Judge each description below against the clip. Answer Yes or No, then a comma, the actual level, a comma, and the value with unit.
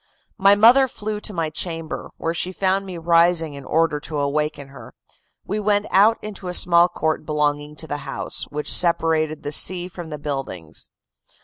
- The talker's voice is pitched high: No, medium, 165 Hz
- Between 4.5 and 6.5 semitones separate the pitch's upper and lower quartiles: No, average, 3.9 semitones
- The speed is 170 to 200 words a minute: Yes, average, 180 wpm